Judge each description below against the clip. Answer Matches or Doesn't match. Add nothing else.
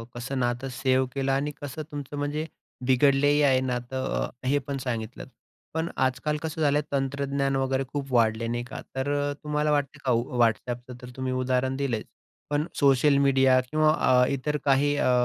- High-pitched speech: Doesn't match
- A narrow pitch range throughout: Matches